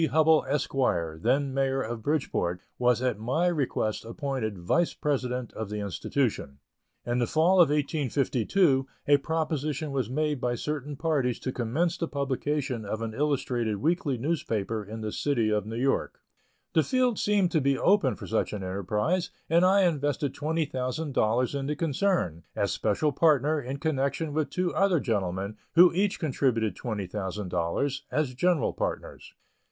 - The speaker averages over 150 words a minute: Yes, average, 160 wpm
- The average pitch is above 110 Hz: Yes, low, 135 Hz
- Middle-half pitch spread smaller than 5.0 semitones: No, wide, 5.5 semitones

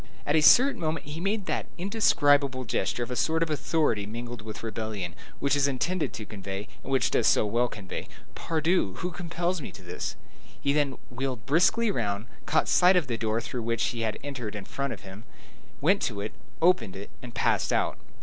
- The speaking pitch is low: Yes, low, 130 Hz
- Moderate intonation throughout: No, wide, 6.7 semitones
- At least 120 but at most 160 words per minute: No, average, 200 wpm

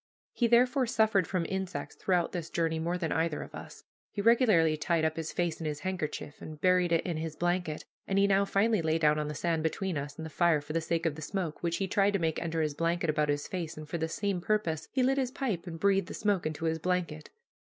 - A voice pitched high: No, medium, 170 Hz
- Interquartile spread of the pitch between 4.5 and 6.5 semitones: No, average, 3.5 semitones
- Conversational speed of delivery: No, fast, 255 wpm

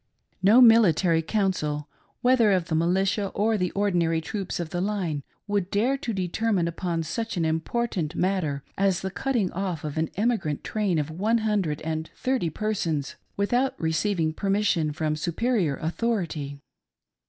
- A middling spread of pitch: Yes, average, 4.7 semitones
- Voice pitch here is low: No, medium, 185 Hz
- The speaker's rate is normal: Yes, average, 150 wpm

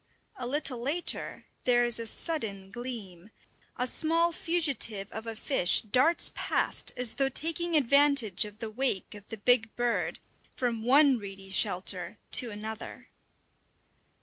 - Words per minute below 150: Yes, average, 140 wpm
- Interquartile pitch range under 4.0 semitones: No, average, 5.0 semitones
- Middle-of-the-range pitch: No, high, 240 Hz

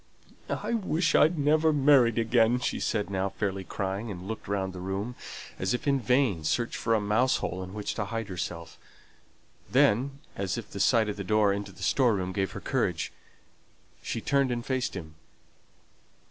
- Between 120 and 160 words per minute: No, average, 185 wpm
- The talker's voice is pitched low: Yes, low, 110 Hz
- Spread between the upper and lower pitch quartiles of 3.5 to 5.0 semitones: Yes, average, 4.5 semitones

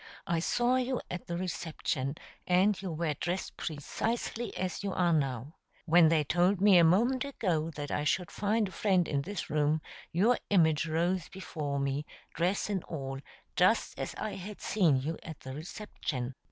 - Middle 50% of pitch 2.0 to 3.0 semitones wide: No, average, 4.5 semitones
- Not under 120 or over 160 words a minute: No, average, 175 wpm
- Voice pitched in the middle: Yes, medium, 175 Hz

